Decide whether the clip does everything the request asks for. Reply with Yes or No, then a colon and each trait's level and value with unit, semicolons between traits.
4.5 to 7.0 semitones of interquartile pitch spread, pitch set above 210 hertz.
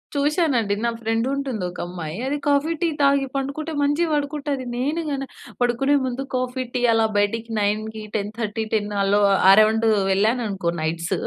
Yes: average, 5.1 semitones; high, 240 Hz